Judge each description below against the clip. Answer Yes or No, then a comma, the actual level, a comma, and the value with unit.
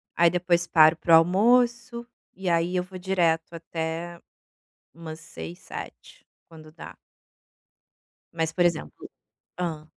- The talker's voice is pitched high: No, medium, 170 Hz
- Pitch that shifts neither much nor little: No, narrow, 1.9 semitones